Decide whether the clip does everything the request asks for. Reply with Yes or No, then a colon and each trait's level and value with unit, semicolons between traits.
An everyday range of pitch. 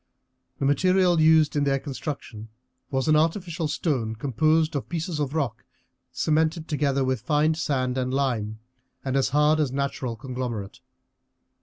Yes: average, 3.4 semitones